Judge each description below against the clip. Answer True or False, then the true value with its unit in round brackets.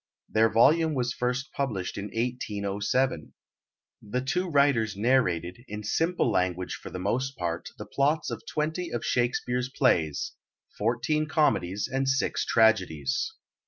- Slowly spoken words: True (130 wpm)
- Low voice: True (120 Hz)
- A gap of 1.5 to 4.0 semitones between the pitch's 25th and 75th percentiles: False (5.1 semitones)